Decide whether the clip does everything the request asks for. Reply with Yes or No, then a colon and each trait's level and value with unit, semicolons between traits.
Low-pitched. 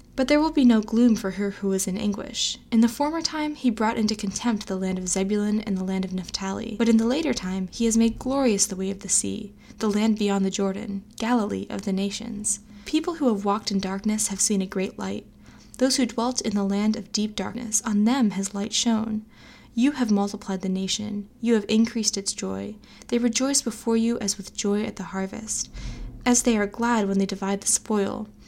No: high, 215 Hz